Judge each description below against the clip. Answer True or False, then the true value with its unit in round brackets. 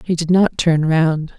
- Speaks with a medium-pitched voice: True (165 Hz)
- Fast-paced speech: True (215 wpm)